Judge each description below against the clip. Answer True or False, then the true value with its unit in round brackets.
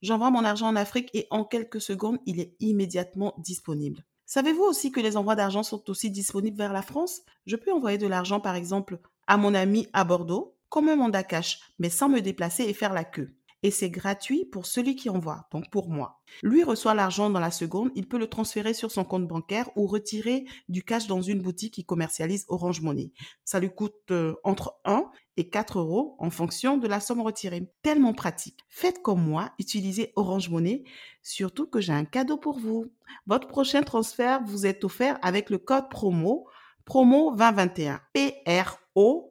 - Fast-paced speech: False (190 wpm)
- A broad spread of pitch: False (4.4 semitones)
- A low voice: False (205 Hz)